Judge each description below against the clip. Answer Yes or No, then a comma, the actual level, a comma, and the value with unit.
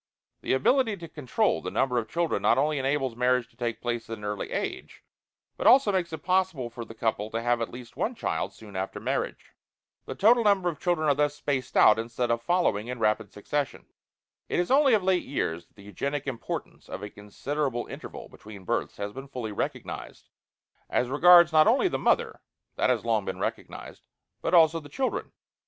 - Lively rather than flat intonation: Yes, wide, 6.9 semitones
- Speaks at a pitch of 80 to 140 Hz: Yes, low, 135 Hz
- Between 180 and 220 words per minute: Yes, average, 200 wpm